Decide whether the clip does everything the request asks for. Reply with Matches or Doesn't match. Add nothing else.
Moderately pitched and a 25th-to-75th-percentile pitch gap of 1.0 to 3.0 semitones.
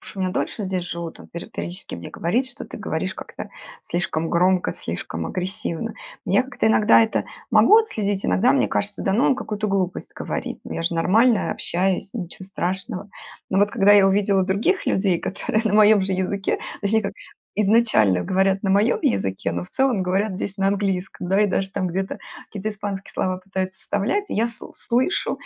Doesn't match